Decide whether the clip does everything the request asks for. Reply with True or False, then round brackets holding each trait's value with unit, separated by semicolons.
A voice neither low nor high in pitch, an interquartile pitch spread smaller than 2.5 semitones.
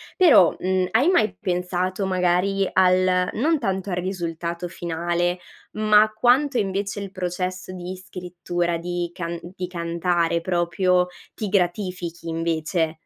True (180 Hz; 2.0 semitones)